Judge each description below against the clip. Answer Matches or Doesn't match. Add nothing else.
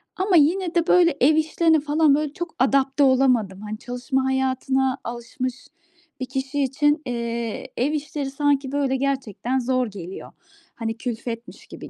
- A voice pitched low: Doesn't match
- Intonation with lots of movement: Doesn't match